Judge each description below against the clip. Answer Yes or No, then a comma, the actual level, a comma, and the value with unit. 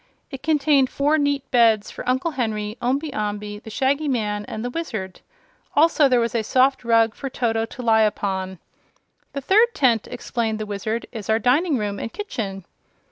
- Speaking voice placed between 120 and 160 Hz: No, high, 235 Hz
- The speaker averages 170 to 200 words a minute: Yes, average, 180 wpm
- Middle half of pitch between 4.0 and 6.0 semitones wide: Yes, average, 4.4 semitones